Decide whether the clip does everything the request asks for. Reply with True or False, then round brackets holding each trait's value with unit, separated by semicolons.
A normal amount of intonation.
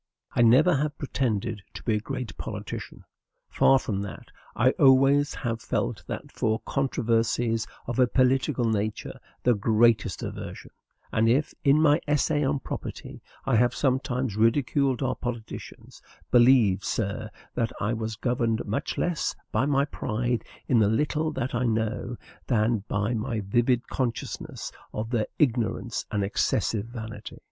True (3.2 semitones)